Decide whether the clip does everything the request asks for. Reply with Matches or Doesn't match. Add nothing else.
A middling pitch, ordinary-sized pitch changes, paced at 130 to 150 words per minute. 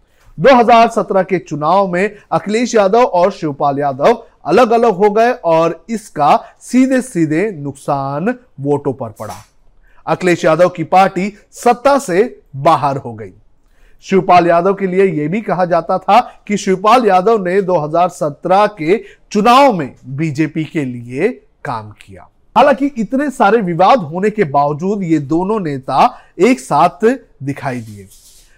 Doesn't match